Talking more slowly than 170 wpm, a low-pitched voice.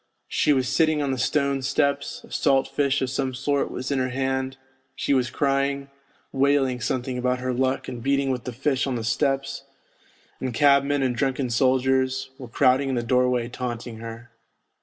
No: average, 180 wpm; low, 130 Hz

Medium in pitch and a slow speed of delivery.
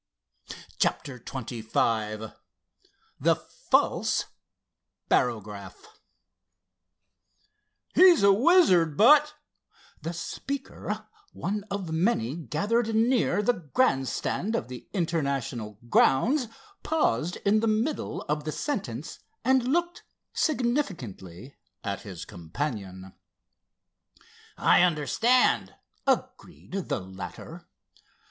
Yes: medium, 170 Hz; slow, 85 wpm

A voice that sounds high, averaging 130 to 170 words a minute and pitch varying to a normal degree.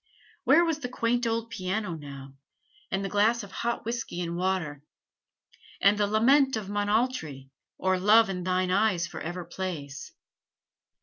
Yes: high, 195 Hz; average, 145 wpm; average, 4.6 semitones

